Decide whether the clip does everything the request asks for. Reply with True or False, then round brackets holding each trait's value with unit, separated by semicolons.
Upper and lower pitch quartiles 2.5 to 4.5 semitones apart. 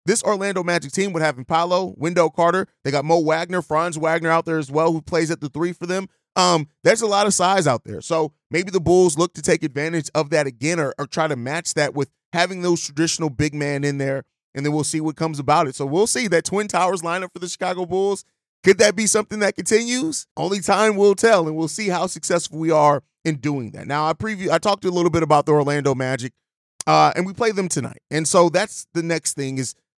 True (3.5 semitones)